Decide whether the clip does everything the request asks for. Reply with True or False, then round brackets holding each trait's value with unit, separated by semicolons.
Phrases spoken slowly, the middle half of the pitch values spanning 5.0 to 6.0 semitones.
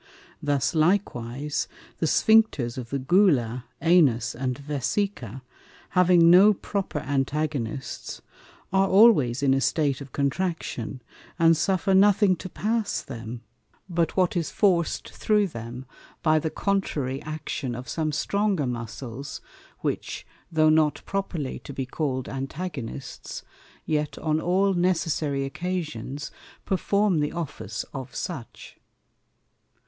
True (120 wpm; 5.6 semitones)